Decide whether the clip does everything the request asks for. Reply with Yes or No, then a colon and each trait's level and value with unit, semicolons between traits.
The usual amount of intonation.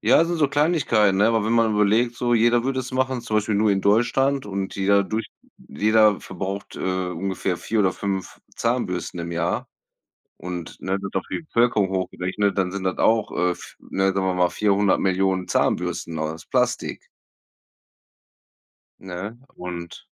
Yes: average, 3.5 semitones